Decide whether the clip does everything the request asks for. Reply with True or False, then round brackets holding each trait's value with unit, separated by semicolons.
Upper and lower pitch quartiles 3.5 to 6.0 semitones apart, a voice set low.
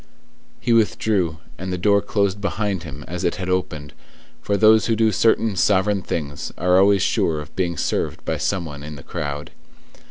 True (4.4 semitones; 95 Hz)